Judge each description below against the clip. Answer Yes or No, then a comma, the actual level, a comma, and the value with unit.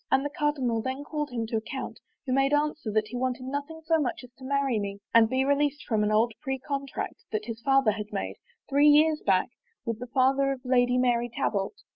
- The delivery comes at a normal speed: No, fast, 220 wpm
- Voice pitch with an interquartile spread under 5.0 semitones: Yes, average, 3.6 semitones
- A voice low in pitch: No, very high, 260 Hz